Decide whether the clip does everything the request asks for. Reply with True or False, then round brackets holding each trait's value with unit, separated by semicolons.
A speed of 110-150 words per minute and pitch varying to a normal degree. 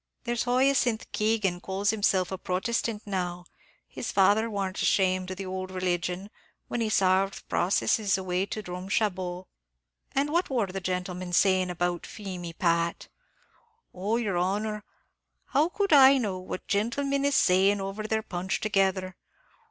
True (145 wpm; 3.1 semitones)